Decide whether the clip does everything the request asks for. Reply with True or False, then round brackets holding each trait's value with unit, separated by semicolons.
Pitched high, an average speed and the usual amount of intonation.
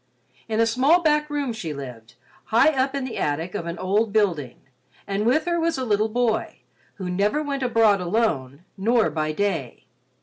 False (220 Hz; 180 wpm; 6.6 semitones)